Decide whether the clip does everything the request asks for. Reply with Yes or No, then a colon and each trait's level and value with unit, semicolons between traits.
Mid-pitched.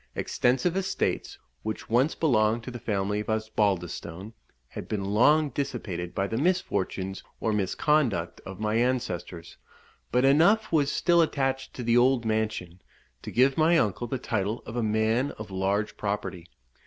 No: low, 110 Hz